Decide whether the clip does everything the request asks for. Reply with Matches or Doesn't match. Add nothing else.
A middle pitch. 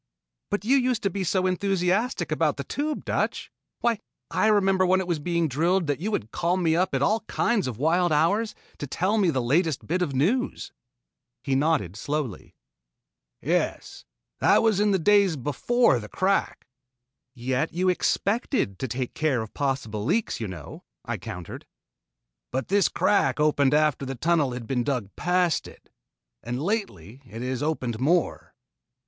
Matches